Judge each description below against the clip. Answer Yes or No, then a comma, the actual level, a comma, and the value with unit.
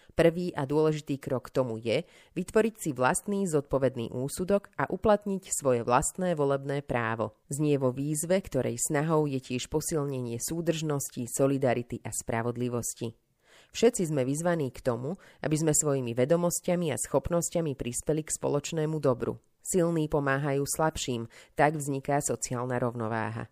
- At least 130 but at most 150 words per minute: Yes, slow, 135 wpm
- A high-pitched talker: No, medium, 140 Hz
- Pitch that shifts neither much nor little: Yes, average, 4.6 semitones